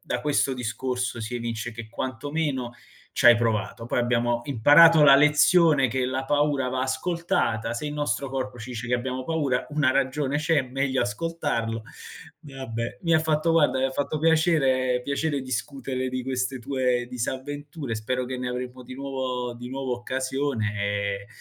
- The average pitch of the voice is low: Yes, low, 130 Hz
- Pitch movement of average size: Yes, average, 3.1 semitones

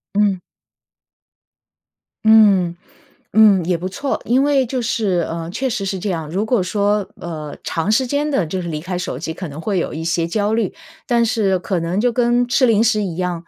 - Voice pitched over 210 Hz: No, high, 200 Hz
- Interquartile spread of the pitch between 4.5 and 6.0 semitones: Yes, average, 4.8 semitones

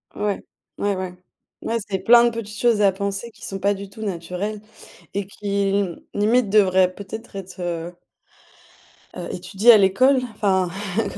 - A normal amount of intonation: No, narrow, 2.1 semitones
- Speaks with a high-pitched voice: Yes, high, 200 Hz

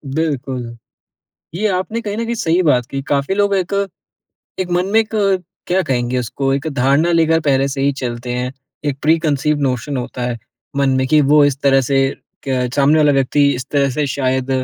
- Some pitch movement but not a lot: Yes, average, 3.8 semitones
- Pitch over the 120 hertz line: Yes, medium, 140 Hz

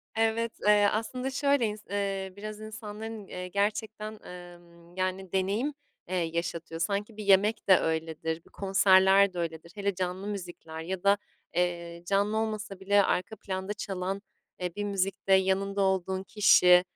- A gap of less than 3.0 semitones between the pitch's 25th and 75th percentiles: Yes, narrow, 2.6 semitones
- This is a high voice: Yes, high, 195 Hz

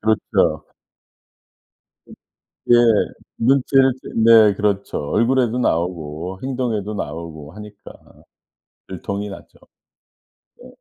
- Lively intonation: No, average, 4.8 semitones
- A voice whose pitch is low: Yes, low, 105 Hz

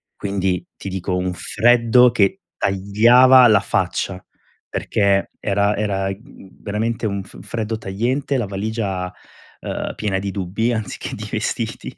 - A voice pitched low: Yes, low, 100 Hz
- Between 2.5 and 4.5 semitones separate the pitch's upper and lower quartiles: Yes, average, 2.9 semitones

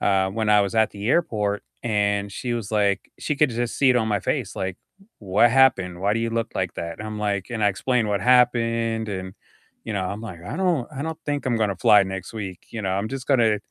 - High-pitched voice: No, low, 110 Hz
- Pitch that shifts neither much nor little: Yes, average, 3.2 semitones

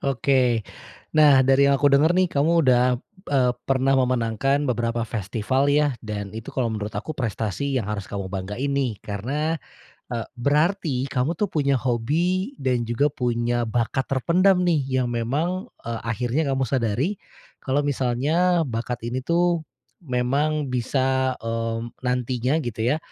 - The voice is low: Yes, low, 130 Hz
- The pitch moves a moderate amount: Yes, average, 3.8 semitones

